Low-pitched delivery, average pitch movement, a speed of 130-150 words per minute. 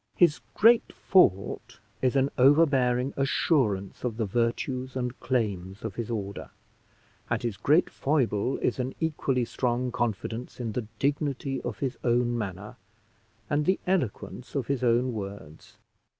Yes: low, 125 Hz; average, 3.6 semitones; average, 140 wpm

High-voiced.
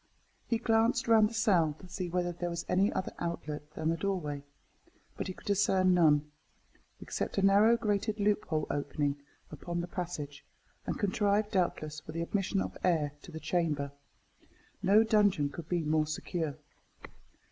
No: medium, 175 Hz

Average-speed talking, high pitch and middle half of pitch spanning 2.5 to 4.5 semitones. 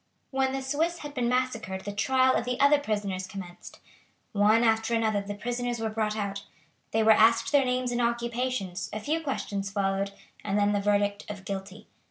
Yes: average, 190 wpm; high, 220 Hz; average, 3.8 semitones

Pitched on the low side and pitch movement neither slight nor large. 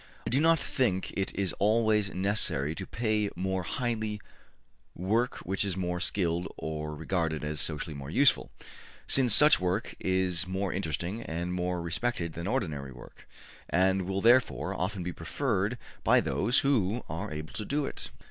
Yes: very low, 95 Hz; average, 4.2 semitones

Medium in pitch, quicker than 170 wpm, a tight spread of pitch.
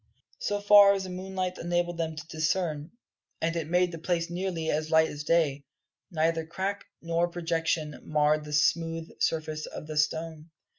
No: medium, 165 Hz; average, 165 wpm; narrow, 2.1 semitones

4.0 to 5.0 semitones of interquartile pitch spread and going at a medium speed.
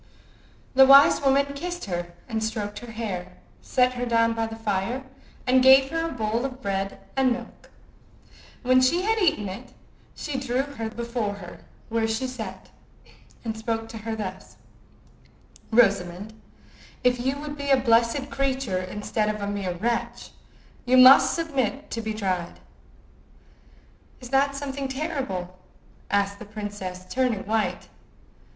Yes: average, 4.4 semitones; average, 145 wpm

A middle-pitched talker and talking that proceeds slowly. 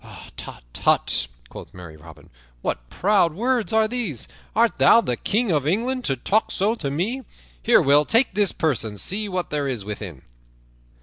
No: medium, 175 Hz; average, 175 wpm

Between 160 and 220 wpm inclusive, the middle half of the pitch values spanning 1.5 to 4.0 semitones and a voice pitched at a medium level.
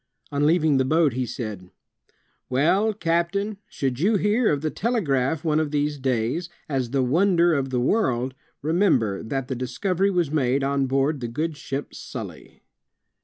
No: average, 165 wpm; average, 4.8 semitones; medium, 145 Hz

